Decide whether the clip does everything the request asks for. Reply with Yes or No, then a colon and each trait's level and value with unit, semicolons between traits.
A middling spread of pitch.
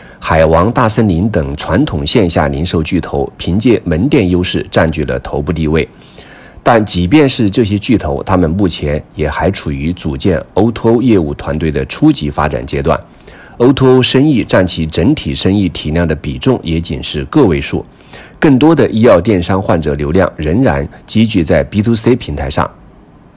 No: wide, 6.6 semitones